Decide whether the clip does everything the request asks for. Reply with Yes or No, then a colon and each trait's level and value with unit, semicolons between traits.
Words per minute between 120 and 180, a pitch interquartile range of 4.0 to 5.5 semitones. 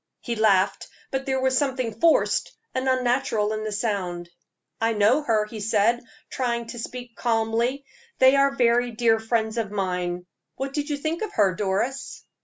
No: average, 170 wpm; average, 3.6 semitones